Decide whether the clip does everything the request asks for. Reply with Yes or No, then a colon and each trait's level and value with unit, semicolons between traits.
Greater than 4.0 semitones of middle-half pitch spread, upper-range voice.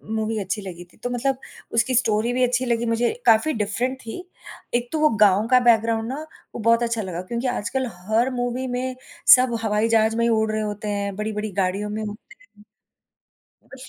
No: narrow, 2.6 semitones; high, 230 Hz